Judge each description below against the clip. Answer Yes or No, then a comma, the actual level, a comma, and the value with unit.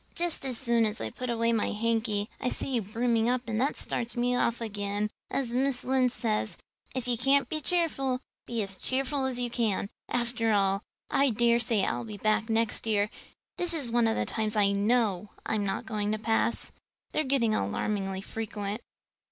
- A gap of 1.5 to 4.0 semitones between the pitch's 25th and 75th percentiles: Yes, average, 2.9 semitones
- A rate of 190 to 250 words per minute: Yes, average, 195 wpm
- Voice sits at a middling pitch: No, high, 230 Hz